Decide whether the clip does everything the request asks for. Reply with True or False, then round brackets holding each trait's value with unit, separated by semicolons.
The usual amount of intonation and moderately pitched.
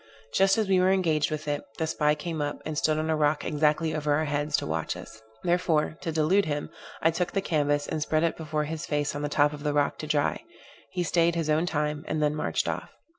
False (1.8 semitones; 155 Hz)